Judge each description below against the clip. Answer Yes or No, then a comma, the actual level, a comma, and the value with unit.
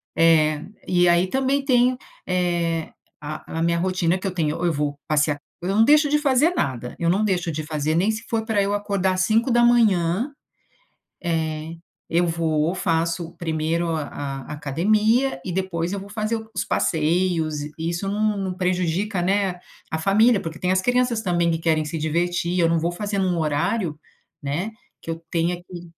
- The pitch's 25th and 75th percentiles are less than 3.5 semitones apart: No, average, 3.9 semitones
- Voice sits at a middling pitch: Yes, medium, 175 Hz